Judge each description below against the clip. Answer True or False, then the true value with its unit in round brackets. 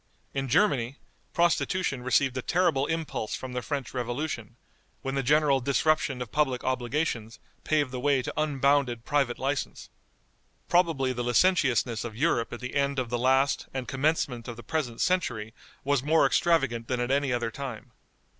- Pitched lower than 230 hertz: True (135 Hz)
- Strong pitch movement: False (3.2 semitones)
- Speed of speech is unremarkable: True (165 wpm)